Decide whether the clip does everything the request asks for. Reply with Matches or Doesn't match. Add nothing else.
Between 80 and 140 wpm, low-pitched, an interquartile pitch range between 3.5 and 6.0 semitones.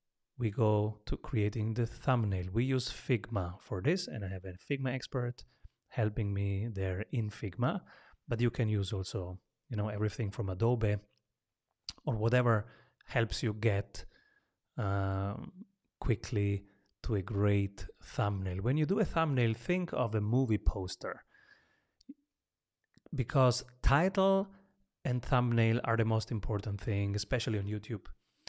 Matches